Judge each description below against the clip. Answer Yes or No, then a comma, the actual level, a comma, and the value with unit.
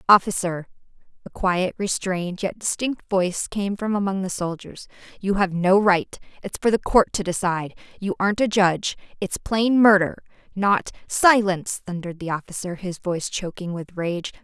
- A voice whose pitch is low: No, high, 190 Hz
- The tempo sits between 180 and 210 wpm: No, average, 150 wpm